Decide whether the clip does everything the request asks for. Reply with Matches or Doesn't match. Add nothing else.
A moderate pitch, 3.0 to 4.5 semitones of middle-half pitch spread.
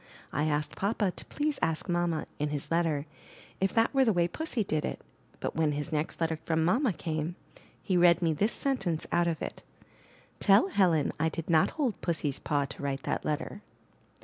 Matches